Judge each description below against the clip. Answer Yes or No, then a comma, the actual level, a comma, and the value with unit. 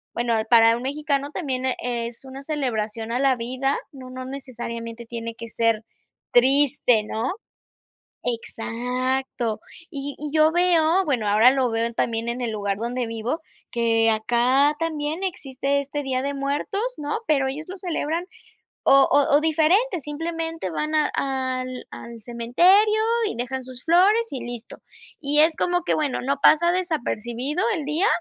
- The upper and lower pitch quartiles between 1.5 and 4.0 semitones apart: No, average, 4.6 semitones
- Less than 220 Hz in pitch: No, very high, 265 Hz